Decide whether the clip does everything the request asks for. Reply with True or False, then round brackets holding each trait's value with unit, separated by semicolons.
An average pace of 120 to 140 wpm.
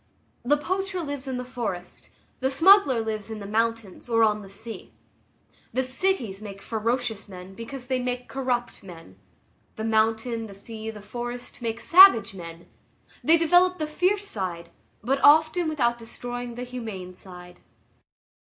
False (155 wpm)